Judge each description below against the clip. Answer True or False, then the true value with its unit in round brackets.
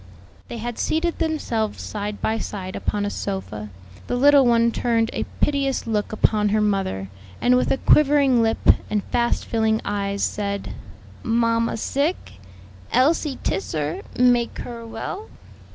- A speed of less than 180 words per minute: True (145 wpm)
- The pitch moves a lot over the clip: False (3.5 semitones)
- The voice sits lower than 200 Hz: False (230 Hz)